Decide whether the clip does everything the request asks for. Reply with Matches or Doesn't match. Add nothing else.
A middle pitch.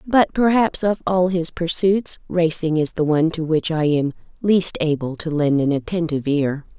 Matches